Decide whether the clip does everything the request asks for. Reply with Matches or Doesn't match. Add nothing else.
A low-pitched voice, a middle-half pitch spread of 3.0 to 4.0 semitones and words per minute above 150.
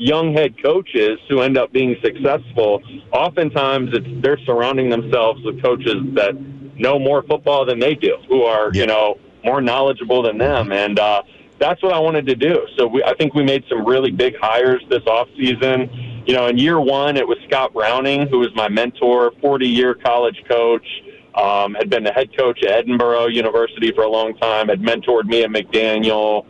Matches